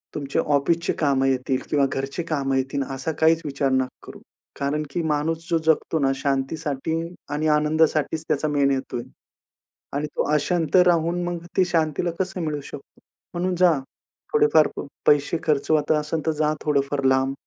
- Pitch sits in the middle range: Yes, medium, 150 Hz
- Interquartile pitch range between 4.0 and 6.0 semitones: No, average, 2.9 semitones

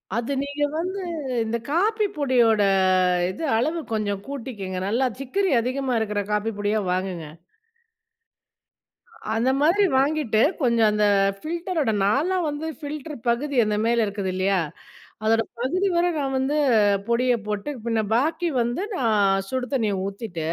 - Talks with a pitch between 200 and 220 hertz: No, high, 240 Hz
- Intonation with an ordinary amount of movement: No, wide, 5.8 semitones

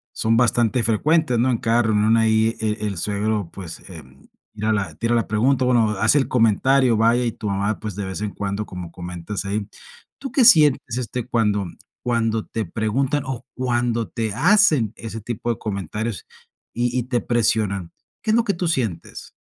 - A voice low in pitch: Yes, low, 115 Hz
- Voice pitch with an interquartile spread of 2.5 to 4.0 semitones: Yes, average, 2.9 semitones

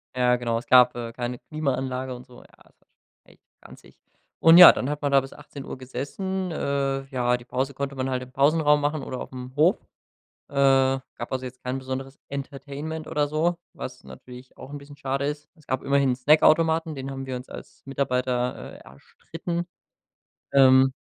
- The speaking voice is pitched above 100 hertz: Yes, low, 135 Hz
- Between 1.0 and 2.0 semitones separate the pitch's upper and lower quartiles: No, narrow, 2.4 semitones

